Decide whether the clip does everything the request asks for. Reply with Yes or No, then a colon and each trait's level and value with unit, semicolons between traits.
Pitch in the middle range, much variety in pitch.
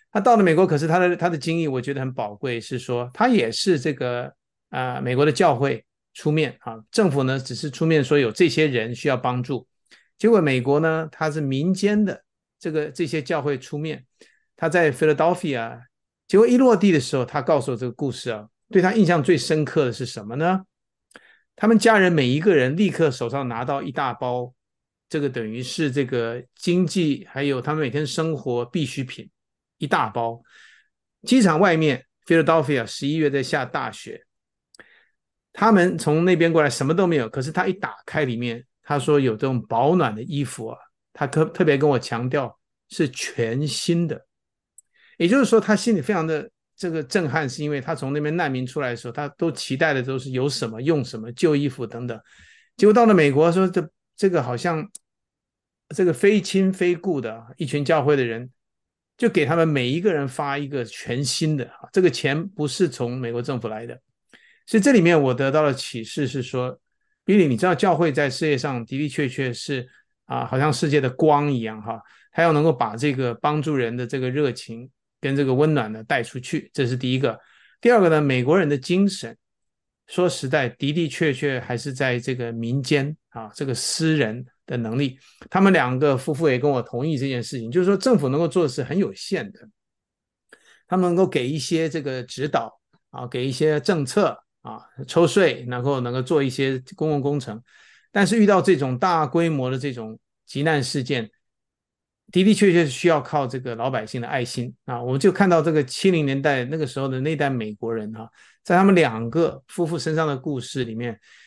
No: medium, 145 Hz; average, 4.8 semitones